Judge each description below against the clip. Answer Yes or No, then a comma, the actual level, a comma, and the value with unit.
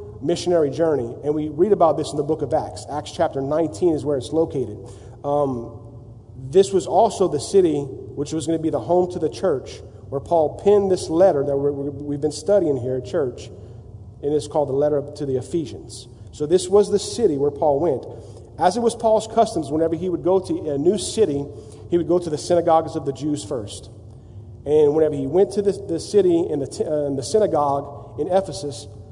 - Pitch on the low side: No, medium, 150 Hz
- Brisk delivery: Yes, fast, 210 wpm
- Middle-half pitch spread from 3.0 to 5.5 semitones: Yes, average, 5.1 semitones